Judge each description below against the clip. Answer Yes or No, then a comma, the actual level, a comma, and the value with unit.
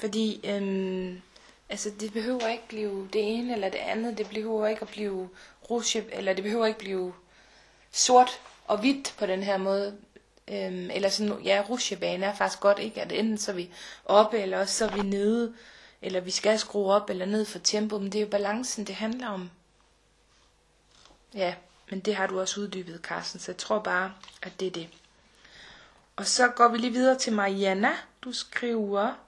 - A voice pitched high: Yes, high, 205 Hz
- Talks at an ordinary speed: Yes, average, 190 wpm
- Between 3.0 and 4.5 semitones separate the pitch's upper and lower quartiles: No, narrow, 2.4 semitones